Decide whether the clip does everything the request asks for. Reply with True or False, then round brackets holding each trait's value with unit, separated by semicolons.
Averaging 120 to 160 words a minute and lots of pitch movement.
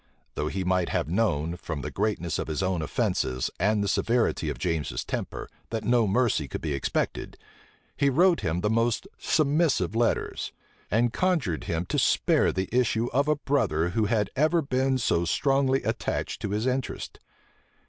False (170 wpm; 7.0 semitones)